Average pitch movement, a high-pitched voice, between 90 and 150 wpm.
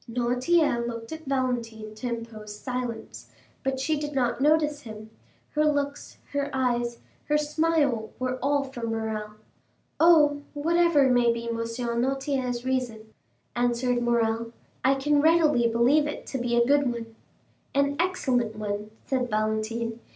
Yes: average, 3.7 semitones; very high, 250 Hz; average, 140 wpm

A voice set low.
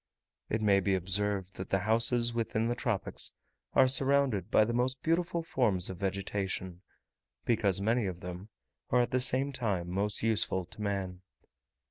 Yes: low, 105 Hz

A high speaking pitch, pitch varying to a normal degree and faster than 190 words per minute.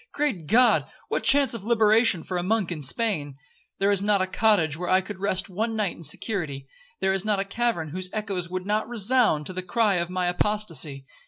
Yes: high, 195 Hz; average, 3.8 semitones; fast, 205 wpm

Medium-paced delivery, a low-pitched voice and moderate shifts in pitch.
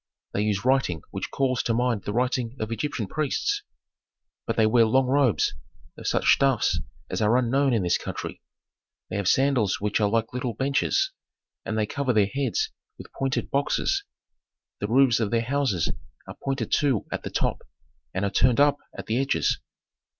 Yes: average, 180 wpm; low, 125 Hz; average, 4.0 semitones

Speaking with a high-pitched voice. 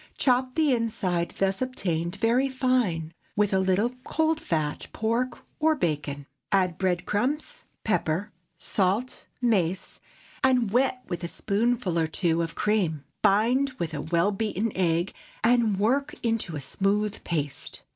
Yes: high, 205 Hz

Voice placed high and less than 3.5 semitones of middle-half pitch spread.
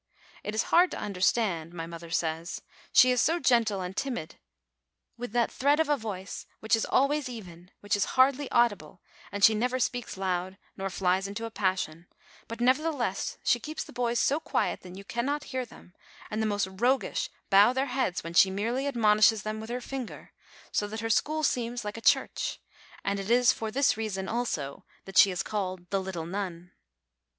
No: high, 215 Hz; average, 4.6 semitones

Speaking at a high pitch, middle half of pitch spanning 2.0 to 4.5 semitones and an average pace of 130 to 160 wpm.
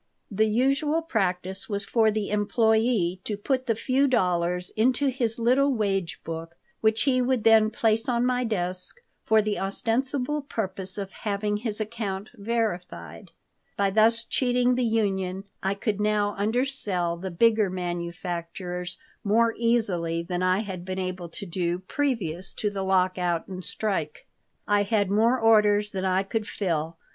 Yes: high, 205 Hz; average, 3.8 semitones; average, 155 wpm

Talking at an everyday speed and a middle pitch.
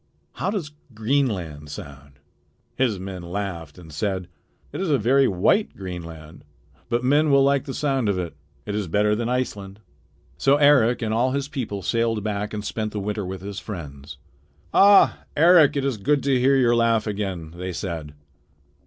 No: average, 175 wpm; low, 105 Hz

